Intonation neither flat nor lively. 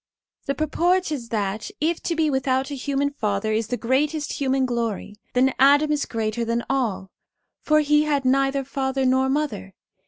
Yes: average, 3.9 semitones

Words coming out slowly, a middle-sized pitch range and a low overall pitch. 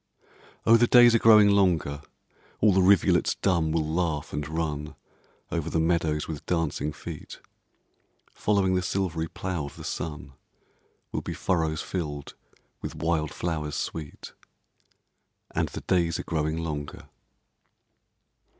Yes: slow, 130 wpm; average, 3.3 semitones; very low, 80 Hz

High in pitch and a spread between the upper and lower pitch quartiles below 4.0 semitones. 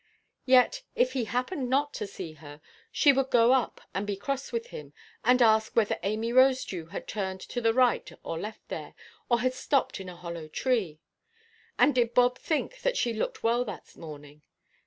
No: high, 235 Hz; average, 4.6 semitones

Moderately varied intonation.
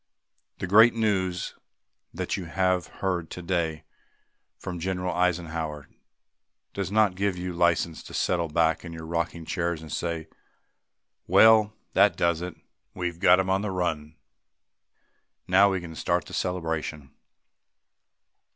No: narrow, 2.3 semitones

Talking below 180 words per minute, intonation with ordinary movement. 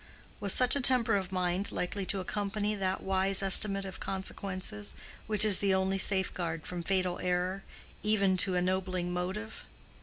No: average, 155 wpm; narrow, 1.6 semitones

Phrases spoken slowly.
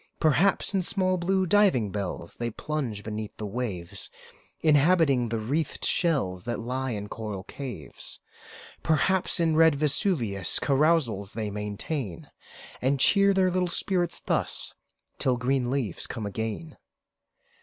Yes: slow, 130 wpm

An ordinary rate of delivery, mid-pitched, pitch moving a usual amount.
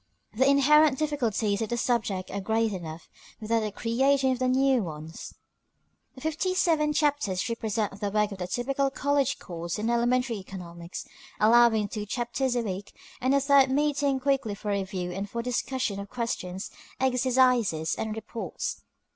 No: average, 160 wpm; high, 235 Hz; average, 4.9 semitones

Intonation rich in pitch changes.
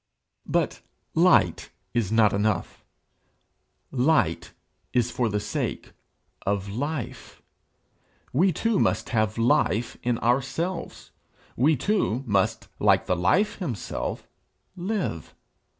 Yes: wide, 7.3 semitones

